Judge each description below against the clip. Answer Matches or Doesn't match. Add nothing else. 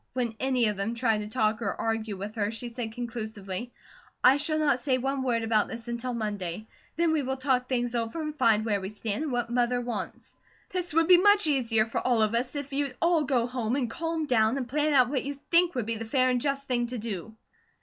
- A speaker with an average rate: Doesn't match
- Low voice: Doesn't match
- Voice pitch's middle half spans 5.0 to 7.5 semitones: Doesn't match